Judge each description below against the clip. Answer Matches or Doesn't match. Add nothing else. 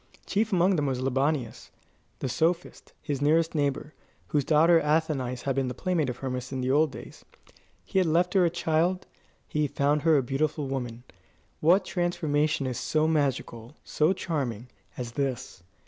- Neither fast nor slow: Matches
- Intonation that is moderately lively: Matches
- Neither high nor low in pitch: Matches